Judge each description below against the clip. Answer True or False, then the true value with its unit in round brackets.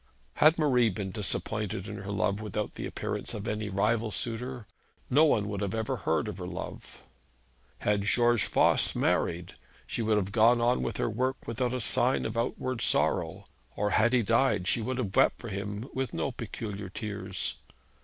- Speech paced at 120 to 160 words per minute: False (185 wpm)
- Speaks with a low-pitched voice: True (110 Hz)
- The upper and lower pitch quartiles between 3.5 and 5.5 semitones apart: False (3.1 semitones)